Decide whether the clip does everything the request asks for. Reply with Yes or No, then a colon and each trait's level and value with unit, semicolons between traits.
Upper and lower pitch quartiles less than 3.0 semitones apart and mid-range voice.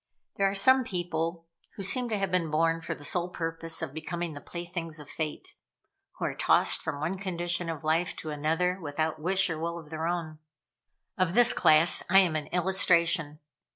Yes: narrow, 2.4 semitones; medium, 170 Hz